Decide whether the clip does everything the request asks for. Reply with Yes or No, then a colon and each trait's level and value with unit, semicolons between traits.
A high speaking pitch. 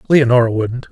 No: low, 125 Hz